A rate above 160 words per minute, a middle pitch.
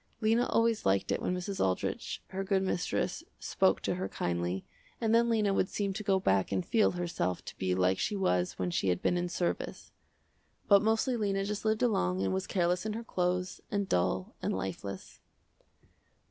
Yes: average, 190 wpm; medium, 180 Hz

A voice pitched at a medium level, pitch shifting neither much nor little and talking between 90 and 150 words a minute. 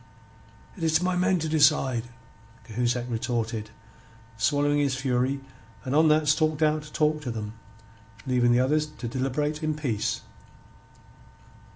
Yes: medium, 145 Hz; average, 3.9 semitones; average, 145 wpm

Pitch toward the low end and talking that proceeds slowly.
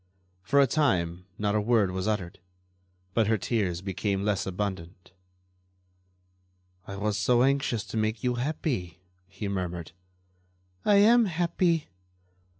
Yes: low, 105 Hz; slow, 130 wpm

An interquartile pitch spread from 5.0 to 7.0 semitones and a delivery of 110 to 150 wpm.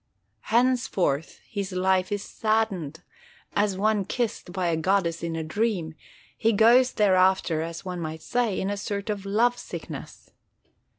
No: average, 4.0 semitones; average, 145 wpm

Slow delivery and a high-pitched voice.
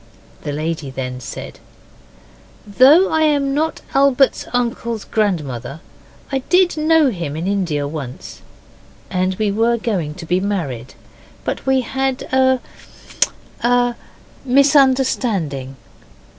Yes: slow, 115 wpm; high, 220 Hz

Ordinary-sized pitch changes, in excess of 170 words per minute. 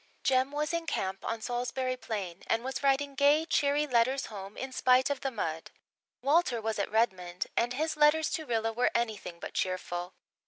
Yes: average, 4.8 semitones; average, 185 wpm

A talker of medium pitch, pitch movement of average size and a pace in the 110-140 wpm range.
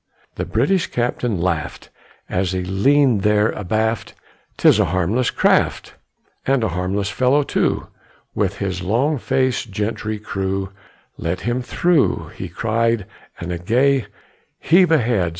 No: low, 110 Hz; average, 4.9 semitones; slow, 135 wpm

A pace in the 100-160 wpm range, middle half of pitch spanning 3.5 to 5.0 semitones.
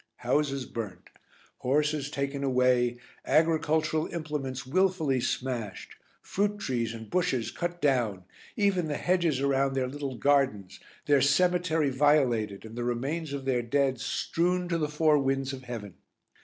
Yes: average, 140 wpm; average, 3.9 semitones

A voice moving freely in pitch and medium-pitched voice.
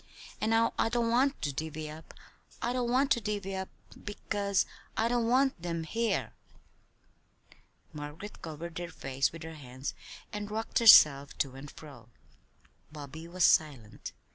Yes: wide, 7.2 semitones; medium, 170 Hz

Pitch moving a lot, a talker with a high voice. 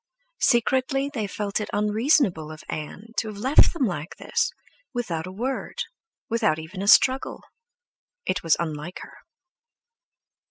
Yes: wide, 6.6 semitones; high, 210 Hz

